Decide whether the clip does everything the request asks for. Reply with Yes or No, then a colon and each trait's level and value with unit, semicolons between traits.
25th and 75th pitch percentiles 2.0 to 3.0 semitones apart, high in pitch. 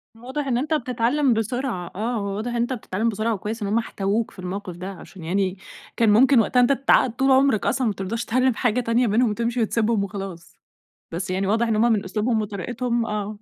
No: average, 3.5 semitones; high, 225 Hz